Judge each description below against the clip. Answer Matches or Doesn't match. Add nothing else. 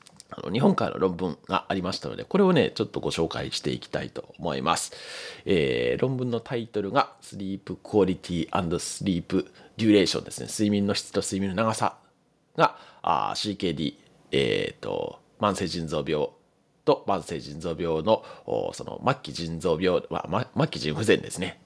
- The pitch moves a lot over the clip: Doesn't match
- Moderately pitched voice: Doesn't match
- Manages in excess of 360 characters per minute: Doesn't match